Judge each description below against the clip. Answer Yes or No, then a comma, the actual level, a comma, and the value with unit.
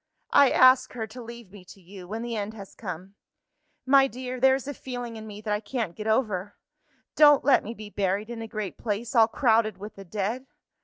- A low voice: No, high, 220 Hz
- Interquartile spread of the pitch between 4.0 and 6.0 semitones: No, average, 3.4 semitones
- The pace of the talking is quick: Yes, fast, 220 wpm